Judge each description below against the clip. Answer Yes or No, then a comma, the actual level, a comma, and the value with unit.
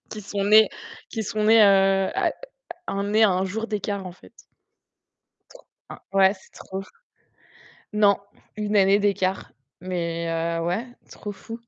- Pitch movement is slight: Yes, narrow, 2.0 semitones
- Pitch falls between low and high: No, high, 200 Hz